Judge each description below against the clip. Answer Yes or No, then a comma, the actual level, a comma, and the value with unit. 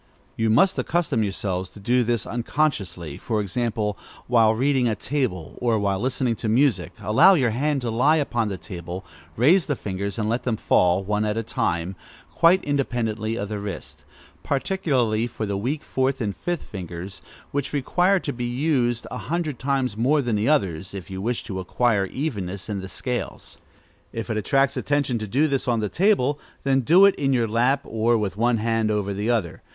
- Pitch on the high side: No, low, 115 Hz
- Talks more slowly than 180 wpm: No, average, 190 wpm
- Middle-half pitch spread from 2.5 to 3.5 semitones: No, average, 4.9 semitones